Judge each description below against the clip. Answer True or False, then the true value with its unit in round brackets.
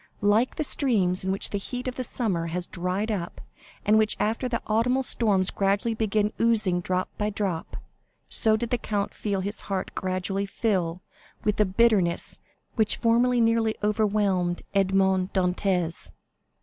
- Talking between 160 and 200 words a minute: False (150 wpm)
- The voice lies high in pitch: True (205 Hz)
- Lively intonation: False (3.3 semitones)